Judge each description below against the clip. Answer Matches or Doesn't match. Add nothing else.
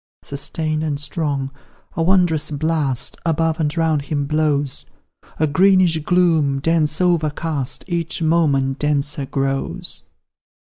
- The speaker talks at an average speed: Doesn't match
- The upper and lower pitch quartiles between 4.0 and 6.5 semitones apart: Doesn't match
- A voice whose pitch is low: Doesn't match